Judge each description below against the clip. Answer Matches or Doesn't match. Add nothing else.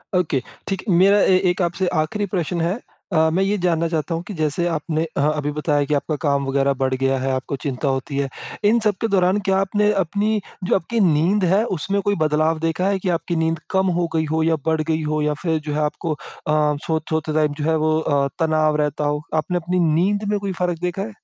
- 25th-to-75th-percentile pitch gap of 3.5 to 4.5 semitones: Matches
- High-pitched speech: Doesn't match